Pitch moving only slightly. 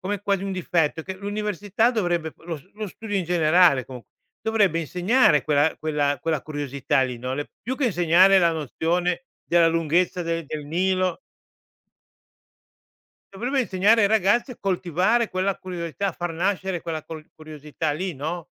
No: average, 4.0 semitones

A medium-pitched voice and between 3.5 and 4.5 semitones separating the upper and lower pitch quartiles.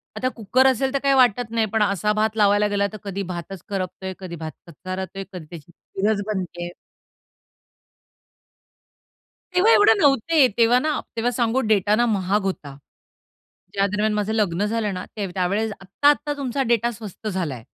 No: high, 210 Hz; average, 3.9 semitones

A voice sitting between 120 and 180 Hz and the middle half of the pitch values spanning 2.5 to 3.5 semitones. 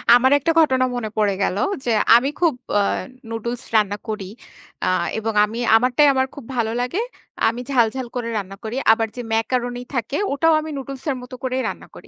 No: high, 245 Hz; average, 2.8 semitones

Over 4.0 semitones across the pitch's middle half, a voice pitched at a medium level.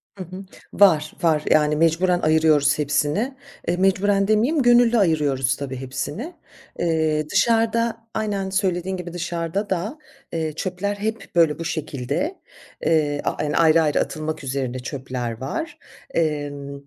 Yes: average, 5.1 semitones; medium, 165 Hz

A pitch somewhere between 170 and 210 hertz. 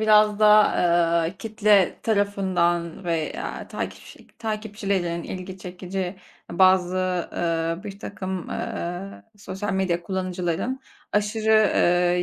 Yes: high, 190 Hz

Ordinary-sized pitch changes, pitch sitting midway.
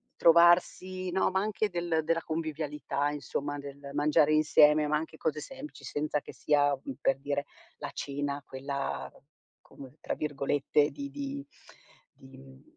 Yes: average, 3.1 semitones; medium, 150 Hz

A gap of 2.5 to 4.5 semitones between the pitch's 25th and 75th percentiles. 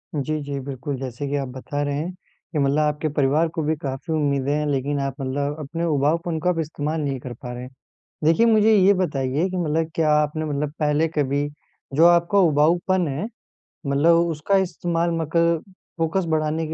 Yes: average, 2.9 semitones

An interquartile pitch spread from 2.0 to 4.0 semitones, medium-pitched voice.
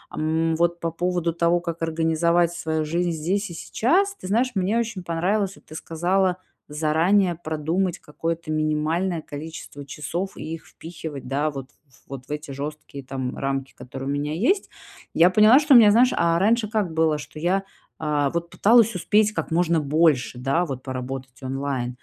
Yes: average, 3.7 semitones; medium, 165 Hz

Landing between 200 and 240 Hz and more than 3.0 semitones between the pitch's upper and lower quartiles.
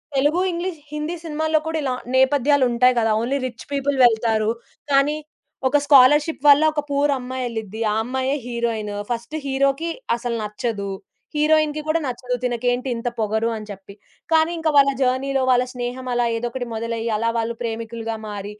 No: very high, 250 Hz; average, 3.7 semitones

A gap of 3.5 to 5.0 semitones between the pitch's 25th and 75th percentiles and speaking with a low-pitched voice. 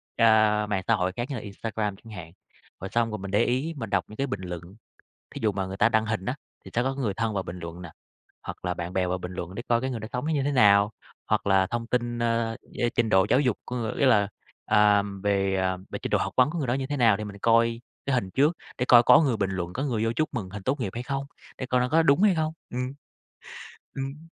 Yes: average, 4.4 semitones; low, 115 Hz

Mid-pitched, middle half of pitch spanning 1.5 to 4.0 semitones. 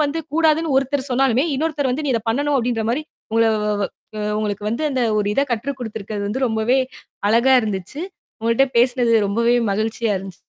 No: high, 240 Hz; average, 3.7 semitones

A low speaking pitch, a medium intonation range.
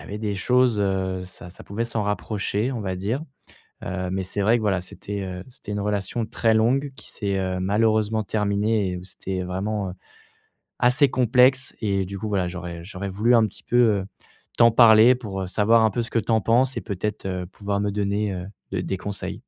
Yes: low, 105 Hz; average, 3.0 semitones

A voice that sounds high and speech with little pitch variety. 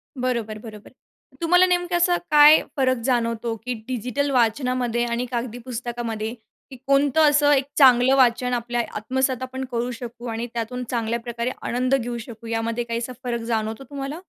Yes: high, 245 Hz; narrow, 2.2 semitones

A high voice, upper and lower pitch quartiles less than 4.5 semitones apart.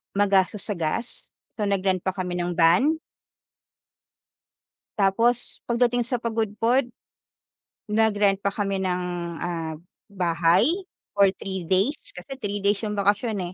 Yes: high, 200 Hz; average, 3.3 semitones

